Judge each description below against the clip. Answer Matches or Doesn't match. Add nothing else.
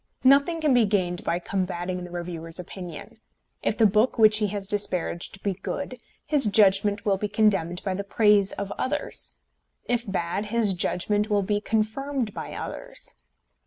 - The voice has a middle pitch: Doesn't match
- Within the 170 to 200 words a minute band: Doesn't match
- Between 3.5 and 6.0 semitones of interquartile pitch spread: Doesn't match